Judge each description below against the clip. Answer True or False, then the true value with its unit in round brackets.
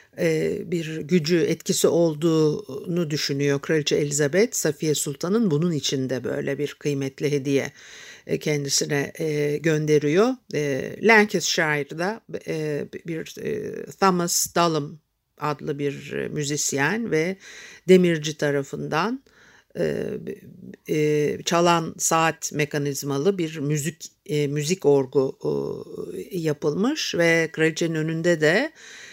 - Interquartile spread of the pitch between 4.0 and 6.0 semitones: False (3.2 semitones)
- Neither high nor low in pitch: True (155 Hz)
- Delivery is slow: True (80 wpm)